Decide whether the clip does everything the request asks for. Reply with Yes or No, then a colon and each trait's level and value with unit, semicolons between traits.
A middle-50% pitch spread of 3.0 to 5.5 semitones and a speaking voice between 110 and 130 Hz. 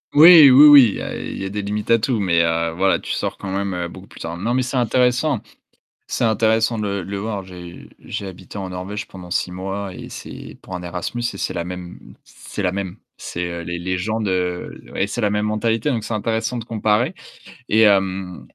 No: average, 3.7 semitones; low, 100 Hz